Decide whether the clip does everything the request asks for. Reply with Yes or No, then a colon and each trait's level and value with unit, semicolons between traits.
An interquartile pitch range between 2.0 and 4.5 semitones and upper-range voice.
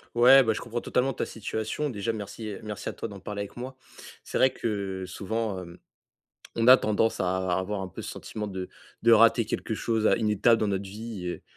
No: average, 2.9 semitones; low, 105 Hz